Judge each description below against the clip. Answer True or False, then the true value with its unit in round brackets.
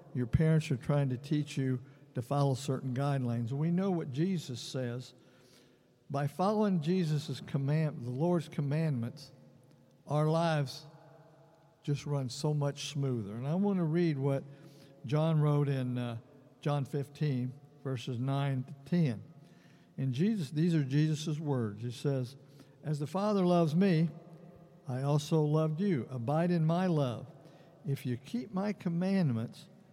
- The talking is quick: False (145 wpm)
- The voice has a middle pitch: True (145 Hz)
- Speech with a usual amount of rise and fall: True (3.6 semitones)